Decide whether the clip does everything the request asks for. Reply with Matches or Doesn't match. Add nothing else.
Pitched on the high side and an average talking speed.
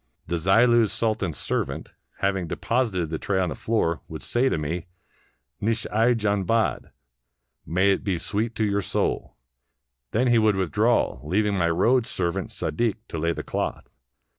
Doesn't match